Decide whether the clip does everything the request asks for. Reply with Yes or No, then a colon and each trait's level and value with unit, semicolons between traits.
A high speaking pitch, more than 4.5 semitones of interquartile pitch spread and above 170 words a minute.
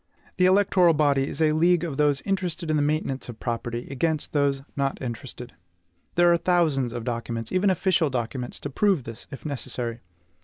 No: medium, 145 Hz; wide, 5.5 semitones; average, 180 wpm